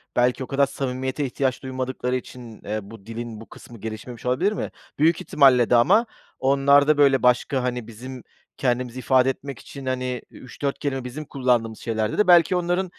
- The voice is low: Yes, low, 130 Hz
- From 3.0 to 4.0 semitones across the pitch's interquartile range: No, narrow, 2.4 semitones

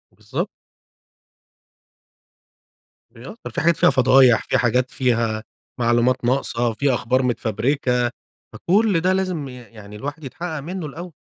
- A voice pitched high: No, low, 130 Hz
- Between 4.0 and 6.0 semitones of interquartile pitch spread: Yes, average, 4.8 semitones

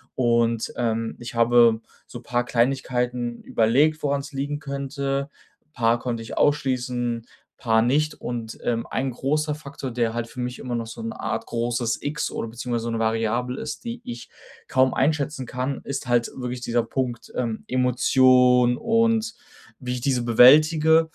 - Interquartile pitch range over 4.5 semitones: No, average, 2.8 semitones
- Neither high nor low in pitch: No, low, 125 Hz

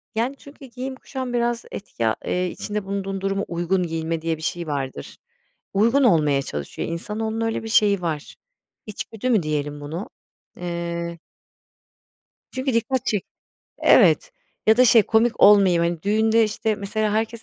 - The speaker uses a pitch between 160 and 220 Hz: Yes, high, 200 Hz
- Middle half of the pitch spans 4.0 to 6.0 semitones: Yes, average, 4.9 semitones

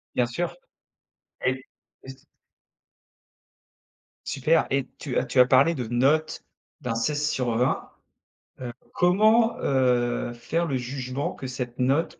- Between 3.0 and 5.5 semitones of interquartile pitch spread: Yes, average, 3.6 semitones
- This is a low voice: Yes, low, 130 Hz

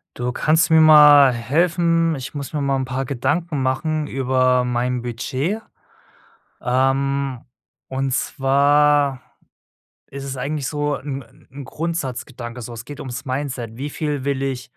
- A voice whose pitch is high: No, low, 135 Hz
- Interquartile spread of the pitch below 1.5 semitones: No, narrow, 2.5 semitones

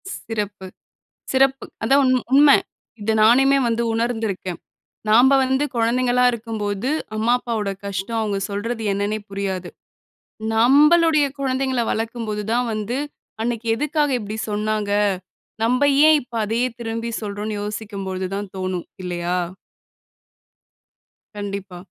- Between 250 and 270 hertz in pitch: No, high, 225 Hz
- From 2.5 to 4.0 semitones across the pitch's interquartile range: Yes, average, 3.5 semitones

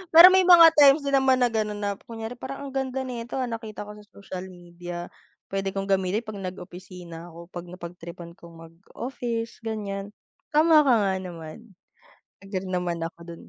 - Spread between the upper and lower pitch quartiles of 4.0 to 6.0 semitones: Yes, wide, 5.6 semitones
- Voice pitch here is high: Yes, high, 200 Hz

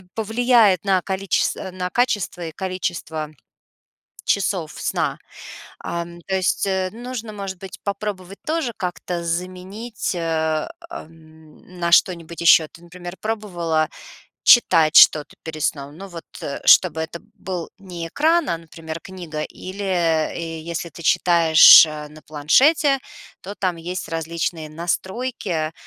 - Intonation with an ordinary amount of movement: Yes, average, 3.3 semitones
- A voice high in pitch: No, medium, 175 Hz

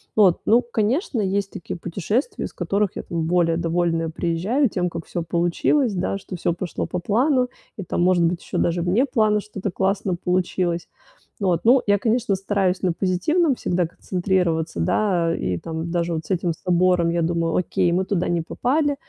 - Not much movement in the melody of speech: No, average, 3.5 semitones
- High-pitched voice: No, medium, 180 Hz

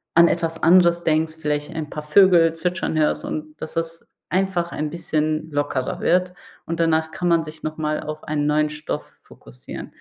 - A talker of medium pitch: Yes, medium, 160 Hz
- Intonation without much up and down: Yes, narrow, 1.9 semitones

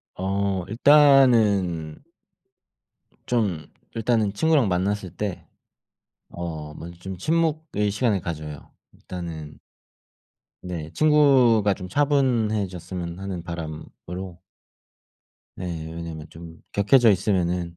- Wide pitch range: No, average, 5.0 semitones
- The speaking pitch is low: Yes, very low, 95 Hz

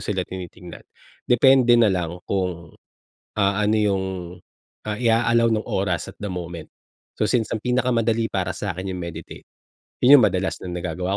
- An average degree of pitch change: Yes, average, 4.1 semitones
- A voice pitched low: Yes, low, 100 Hz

